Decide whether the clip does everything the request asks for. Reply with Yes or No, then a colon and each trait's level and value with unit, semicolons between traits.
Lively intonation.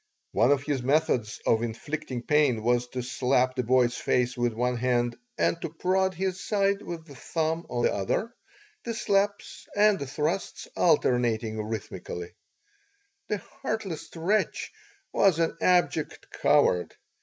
Yes: wide, 6.7 semitones